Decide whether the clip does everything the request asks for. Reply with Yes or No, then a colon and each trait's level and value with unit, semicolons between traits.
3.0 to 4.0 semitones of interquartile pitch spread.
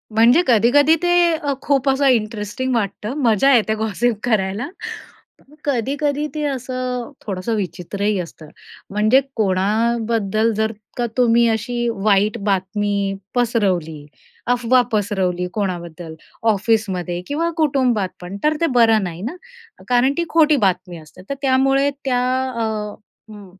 No: average, 4.5 semitones